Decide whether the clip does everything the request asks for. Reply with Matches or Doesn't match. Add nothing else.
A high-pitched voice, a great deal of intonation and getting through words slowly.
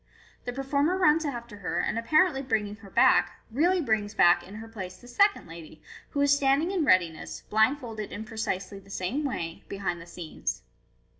Doesn't match